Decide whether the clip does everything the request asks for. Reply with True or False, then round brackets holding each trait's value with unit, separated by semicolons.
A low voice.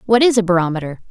False (195 Hz)